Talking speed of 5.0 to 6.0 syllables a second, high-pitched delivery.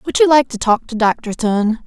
No: 4.6 syllables/s; high, 240 Hz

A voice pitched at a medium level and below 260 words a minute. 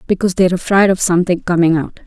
Yes: medium, 180 Hz; fast, 205 wpm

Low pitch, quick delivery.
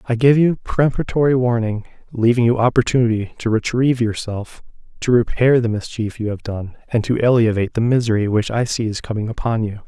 No: low, 115 Hz; average, 180 wpm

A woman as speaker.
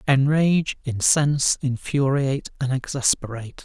No: male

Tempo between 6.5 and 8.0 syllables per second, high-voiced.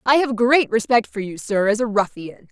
No: 5.0 syllables/s; high, 225 Hz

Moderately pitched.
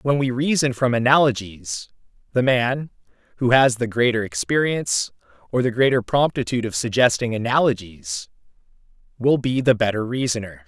No: low, 120 Hz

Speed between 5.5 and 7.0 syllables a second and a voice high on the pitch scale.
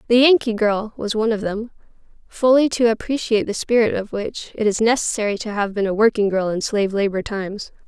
Yes: 5.9 syllables/s; high, 215 Hz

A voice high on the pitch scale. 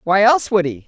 Yes: high, 200 Hz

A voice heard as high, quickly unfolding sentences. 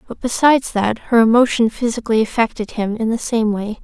No: high, 225 Hz; average, 190 wpm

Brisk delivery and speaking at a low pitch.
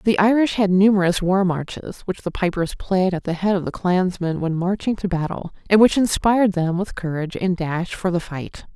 No: fast, 210 wpm; medium, 185 Hz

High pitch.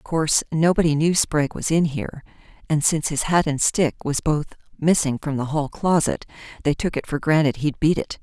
No: medium, 155 Hz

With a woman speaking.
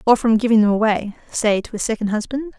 Yes: female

